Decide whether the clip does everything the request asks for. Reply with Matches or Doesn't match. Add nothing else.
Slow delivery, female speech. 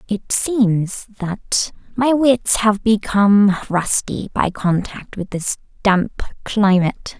Matches